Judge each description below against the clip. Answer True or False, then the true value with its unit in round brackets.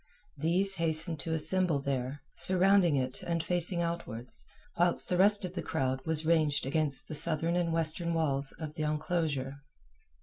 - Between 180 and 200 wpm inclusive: False (160 wpm)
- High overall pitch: False (160 Hz)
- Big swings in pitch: False (3.2 semitones)